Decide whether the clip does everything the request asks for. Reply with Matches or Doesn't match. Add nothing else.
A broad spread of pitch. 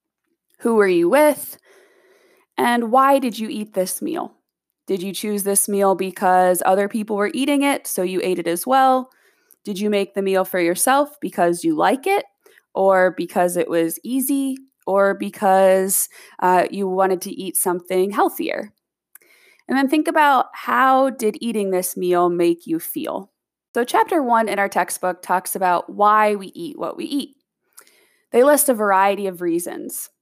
Matches